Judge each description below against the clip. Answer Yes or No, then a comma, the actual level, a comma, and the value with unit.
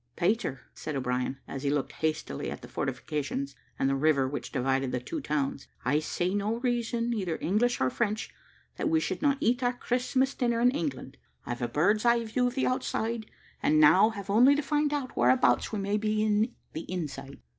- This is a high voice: Yes, high, 205 Hz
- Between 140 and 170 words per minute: No, average, 200 wpm